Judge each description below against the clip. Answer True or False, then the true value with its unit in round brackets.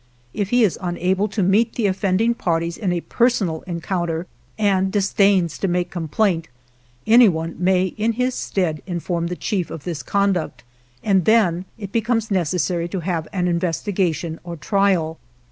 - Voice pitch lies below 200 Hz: True (185 Hz)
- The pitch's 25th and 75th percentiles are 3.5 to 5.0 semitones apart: False (3.1 semitones)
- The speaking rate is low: False (155 wpm)